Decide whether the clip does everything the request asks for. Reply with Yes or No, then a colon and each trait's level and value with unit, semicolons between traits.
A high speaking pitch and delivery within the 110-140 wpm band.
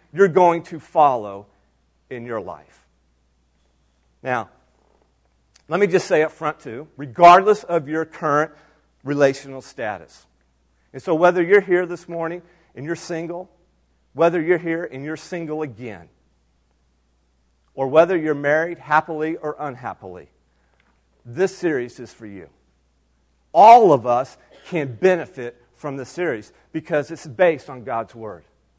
No: medium, 140 Hz; slow, 135 wpm